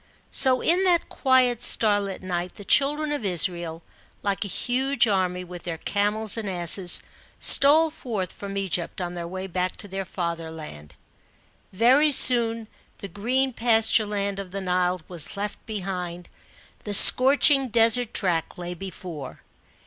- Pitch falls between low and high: No, high, 200 Hz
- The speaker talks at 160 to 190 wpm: No, average, 145 wpm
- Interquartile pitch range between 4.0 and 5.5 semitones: Yes, average, 5.0 semitones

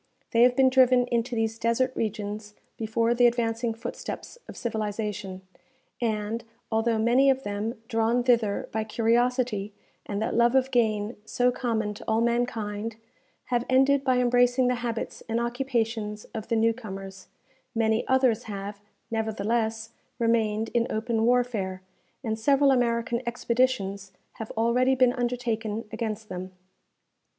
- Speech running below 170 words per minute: Yes, average, 140 wpm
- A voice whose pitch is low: No, high, 230 Hz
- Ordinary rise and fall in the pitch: No, narrow, 2.2 semitones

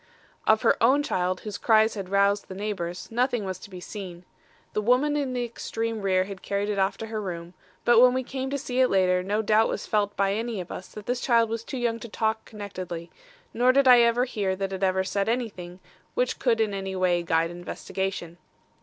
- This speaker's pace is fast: Yes, fast, 225 wpm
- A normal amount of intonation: Yes, average, 3.8 semitones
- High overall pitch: Yes, high, 205 Hz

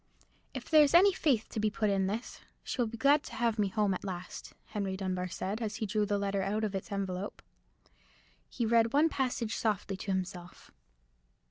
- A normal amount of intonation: Yes, average, 3.2 semitones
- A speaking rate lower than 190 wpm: No, average, 200 wpm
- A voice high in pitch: Yes, high, 210 Hz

